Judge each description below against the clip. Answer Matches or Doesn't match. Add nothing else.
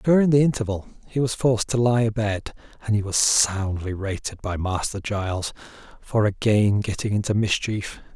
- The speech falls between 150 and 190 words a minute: Matches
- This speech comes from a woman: Doesn't match